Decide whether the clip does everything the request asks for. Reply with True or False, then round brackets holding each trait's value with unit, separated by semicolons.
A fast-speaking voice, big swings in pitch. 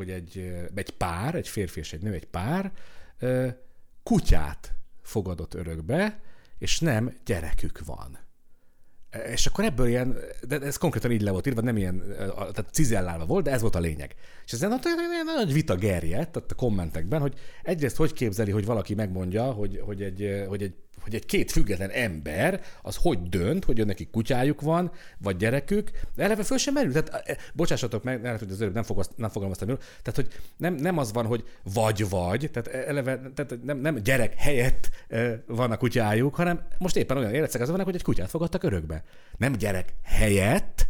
True (175 wpm; 7.0 semitones)